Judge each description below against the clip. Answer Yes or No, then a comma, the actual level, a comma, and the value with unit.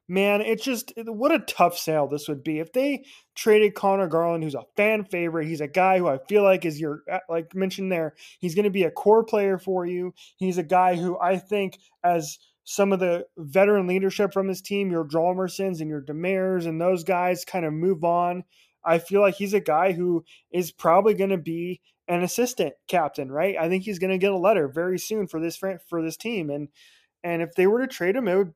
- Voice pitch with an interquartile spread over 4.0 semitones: No, average, 2.8 semitones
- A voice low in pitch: No, medium, 185 Hz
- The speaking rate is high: Yes, fast, 225 wpm